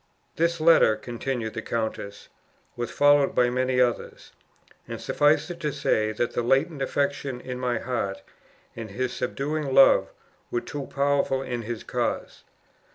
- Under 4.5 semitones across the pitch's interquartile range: Yes, average, 3.1 semitones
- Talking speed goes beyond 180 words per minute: No, average, 150 wpm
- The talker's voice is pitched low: Yes, low, 130 Hz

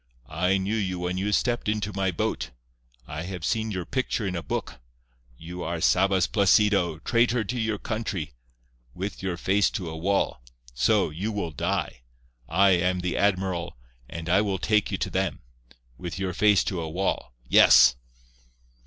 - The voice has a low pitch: Yes, very low, 95 Hz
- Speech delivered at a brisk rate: No, average, 170 wpm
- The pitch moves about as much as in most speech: Yes, average, 3.0 semitones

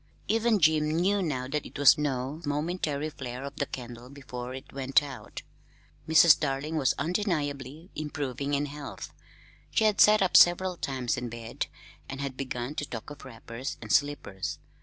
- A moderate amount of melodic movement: Yes, average, 3.4 semitones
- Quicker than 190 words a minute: No, average, 165 wpm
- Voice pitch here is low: No, medium, 145 Hz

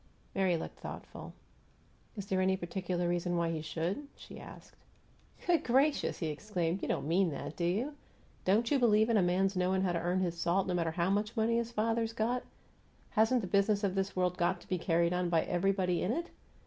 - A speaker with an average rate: No, fast, 210 wpm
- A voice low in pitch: No, high, 190 Hz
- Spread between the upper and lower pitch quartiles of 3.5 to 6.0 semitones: Yes, average, 3.8 semitones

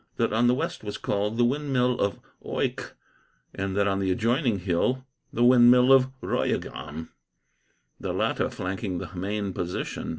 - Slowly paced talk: No, average, 155 wpm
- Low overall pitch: Yes, low, 105 Hz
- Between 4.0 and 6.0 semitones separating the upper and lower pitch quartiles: Yes, average, 4.5 semitones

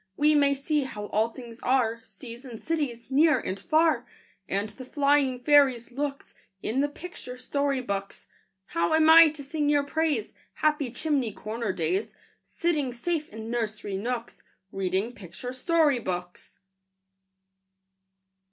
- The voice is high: Yes, very high, 255 Hz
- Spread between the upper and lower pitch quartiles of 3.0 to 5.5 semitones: Yes, average, 4.8 semitones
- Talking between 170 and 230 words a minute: No, average, 140 wpm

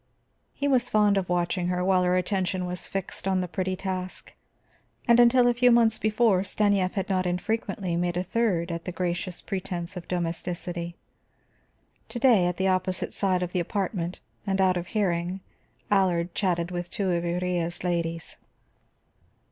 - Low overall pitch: No, medium, 185 Hz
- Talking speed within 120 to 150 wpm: No, average, 165 wpm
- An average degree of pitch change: No, narrow, 2.0 semitones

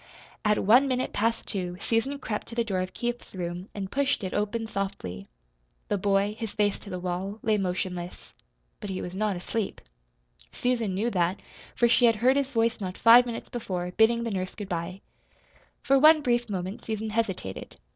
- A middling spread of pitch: Yes, average, 3.9 semitones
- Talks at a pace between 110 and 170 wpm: No, average, 185 wpm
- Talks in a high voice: Yes, high, 210 Hz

